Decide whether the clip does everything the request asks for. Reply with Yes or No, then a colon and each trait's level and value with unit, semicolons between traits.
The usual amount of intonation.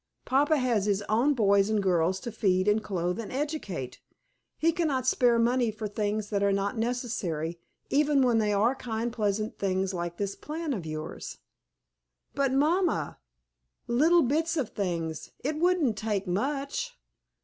No: wide, 5.7 semitones